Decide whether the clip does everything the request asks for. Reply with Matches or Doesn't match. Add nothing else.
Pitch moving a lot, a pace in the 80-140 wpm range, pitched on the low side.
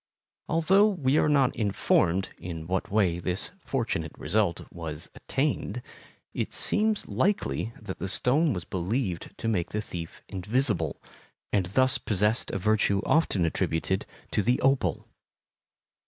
Matches